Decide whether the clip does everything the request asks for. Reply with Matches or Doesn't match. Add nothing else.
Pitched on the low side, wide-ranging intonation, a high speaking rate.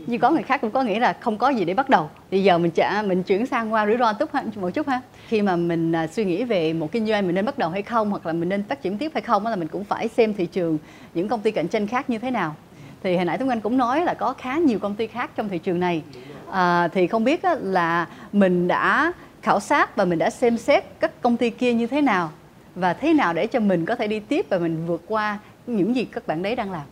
Doesn't match